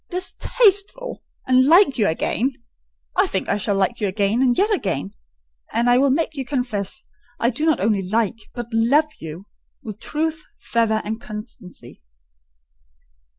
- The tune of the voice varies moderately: No, wide, 6.4 semitones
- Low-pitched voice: No, high, 240 Hz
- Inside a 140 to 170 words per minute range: Yes, average, 145 wpm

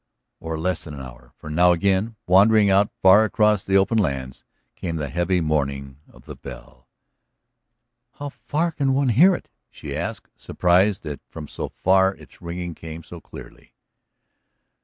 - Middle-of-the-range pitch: No, very low, 90 Hz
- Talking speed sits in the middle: Yes, average, 160 wpm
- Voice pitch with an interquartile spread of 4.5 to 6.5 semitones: Yes, average, 5.0 semitones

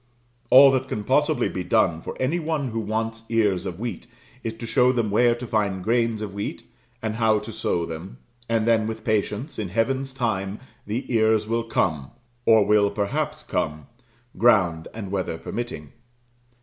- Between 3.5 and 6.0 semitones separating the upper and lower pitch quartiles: No, average, 2.8 semitones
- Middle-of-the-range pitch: No, low, 110 Hz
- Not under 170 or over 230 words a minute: Yes, average, 175 wpm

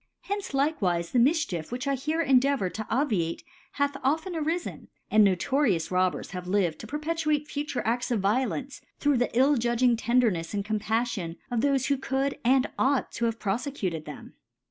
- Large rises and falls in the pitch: Yes, wide, 5.7 semitones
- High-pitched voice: Yes, high, 245 Hz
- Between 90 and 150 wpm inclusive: No, average, 170 wpm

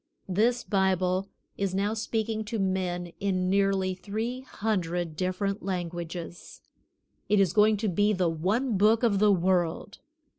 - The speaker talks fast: No, average, 140 wpm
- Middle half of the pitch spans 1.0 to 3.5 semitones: Yes, average, 2.7 semitones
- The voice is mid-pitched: No, high, 195 Hz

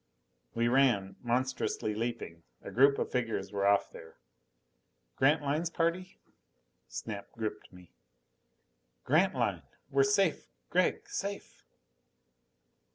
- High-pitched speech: No, low, 125 Hz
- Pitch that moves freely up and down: Yes, wide, 7.8 semitones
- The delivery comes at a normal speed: No, slow, 95 wpm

